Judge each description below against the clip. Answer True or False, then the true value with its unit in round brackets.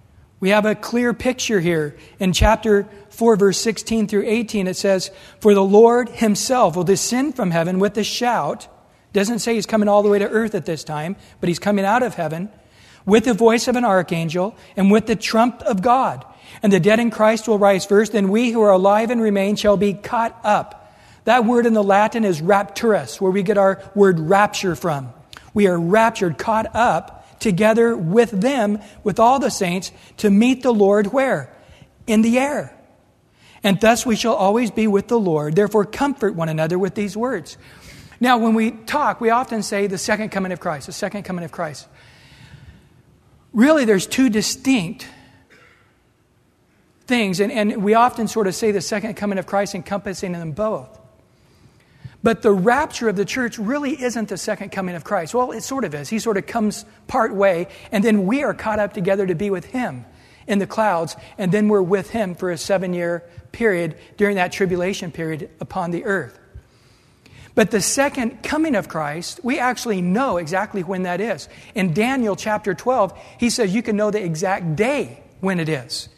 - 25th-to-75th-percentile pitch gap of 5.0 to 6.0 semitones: False (3.1 semitones)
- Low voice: False (205 Hz)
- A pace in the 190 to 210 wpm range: True (195 wpm)